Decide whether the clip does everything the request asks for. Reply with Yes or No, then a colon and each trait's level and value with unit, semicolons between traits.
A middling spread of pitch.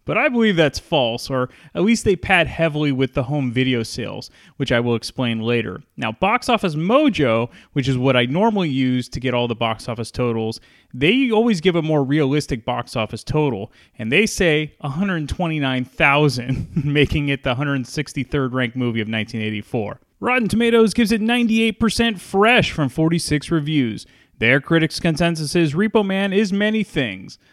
No: wide, 7.3 semitones